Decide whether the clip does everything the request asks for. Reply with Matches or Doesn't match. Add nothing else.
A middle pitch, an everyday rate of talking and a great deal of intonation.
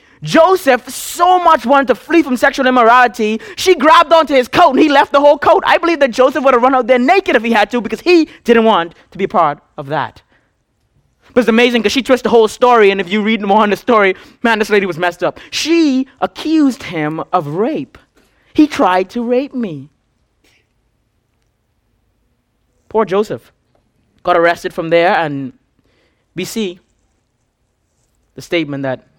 Doesn't match